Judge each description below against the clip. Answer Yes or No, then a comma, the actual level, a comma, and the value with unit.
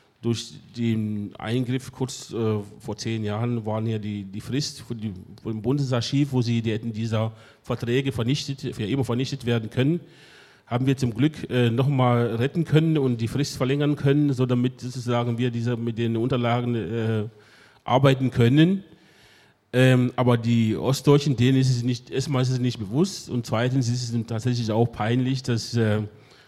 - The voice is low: Yes, low, 125 Hz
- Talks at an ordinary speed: Yes, average, 170 wpm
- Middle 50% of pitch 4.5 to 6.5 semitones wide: No, narrow, 2.6 semitones